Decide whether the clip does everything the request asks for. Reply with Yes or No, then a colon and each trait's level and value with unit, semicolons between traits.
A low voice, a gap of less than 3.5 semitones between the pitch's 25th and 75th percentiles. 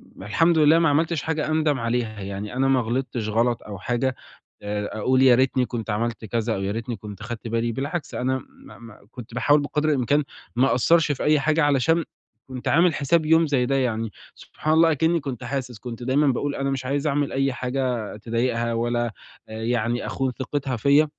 No: low, 130 Hz; average, 3.9 semitones